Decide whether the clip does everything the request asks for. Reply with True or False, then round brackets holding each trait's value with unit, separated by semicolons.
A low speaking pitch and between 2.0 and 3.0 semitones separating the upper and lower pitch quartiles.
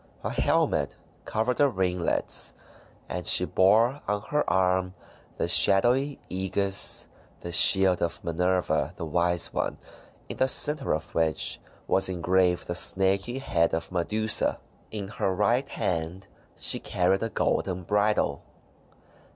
False (95 Hz; 3.4 semitones)